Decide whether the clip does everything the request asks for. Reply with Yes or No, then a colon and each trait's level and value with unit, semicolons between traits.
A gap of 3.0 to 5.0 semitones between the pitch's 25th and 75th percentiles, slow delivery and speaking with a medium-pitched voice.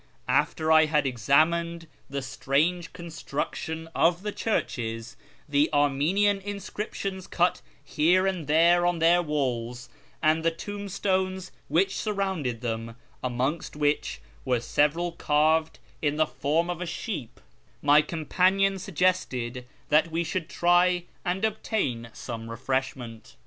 Yes: average, 4.5 semitones; slow, 125 wpm; medium, 160 Hz